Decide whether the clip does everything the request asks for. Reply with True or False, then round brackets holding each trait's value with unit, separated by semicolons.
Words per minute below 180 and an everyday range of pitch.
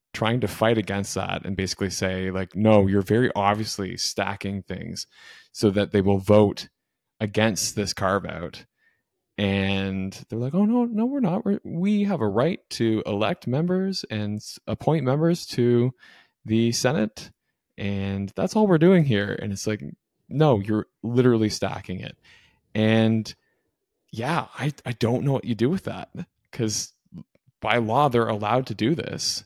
True (160 wpm; 4.3 semitones)